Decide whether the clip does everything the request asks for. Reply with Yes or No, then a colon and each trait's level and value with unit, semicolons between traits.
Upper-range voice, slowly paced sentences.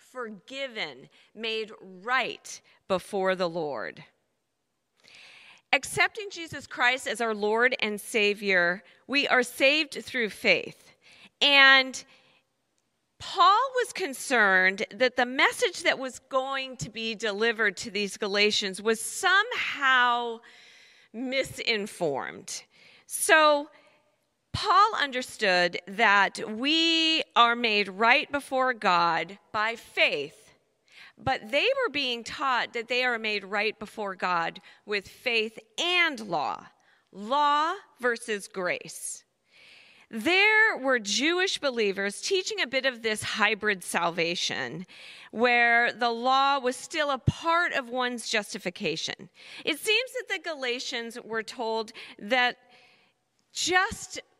Yes: high, 245 Hz; slow, 110 wpm